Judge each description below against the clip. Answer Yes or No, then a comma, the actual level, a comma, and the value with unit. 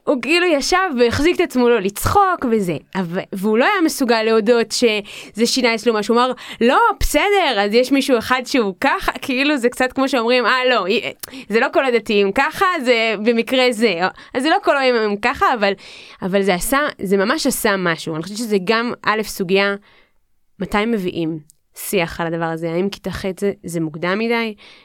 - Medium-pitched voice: No, high, 230 Hz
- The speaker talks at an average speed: No, fast, 185 wpm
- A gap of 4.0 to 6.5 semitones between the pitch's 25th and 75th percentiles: Yes, average, 4.8 semitones